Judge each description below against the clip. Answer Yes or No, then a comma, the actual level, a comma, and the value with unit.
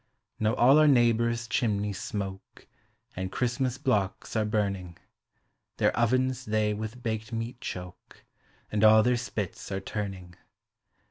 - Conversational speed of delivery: No, slow, 130 wpm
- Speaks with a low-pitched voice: Yes, low, 110 Hz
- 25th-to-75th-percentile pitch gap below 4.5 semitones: Yes, average, 3.1 semitones